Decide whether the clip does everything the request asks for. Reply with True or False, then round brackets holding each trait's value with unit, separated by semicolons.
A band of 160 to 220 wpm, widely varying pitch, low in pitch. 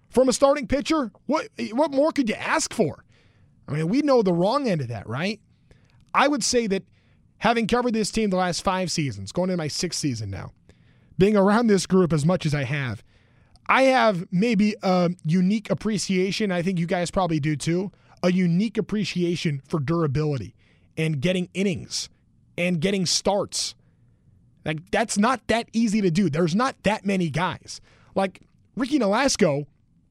False (175 wpm; 5.7 semitones; 185 Hz)